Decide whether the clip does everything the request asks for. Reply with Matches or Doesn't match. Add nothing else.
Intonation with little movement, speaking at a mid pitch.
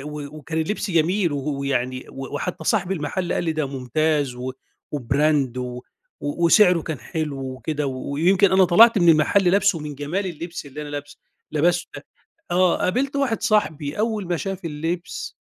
Doesn't match